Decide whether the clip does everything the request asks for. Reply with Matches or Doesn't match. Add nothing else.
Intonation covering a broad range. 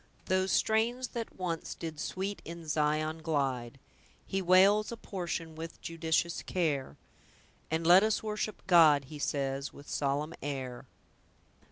Doesn't match